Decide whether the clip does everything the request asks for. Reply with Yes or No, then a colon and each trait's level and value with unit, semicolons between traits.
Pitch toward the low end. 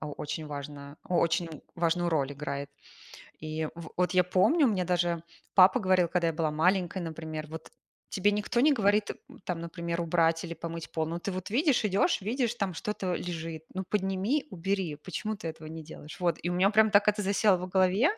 No: medium, 175 Hz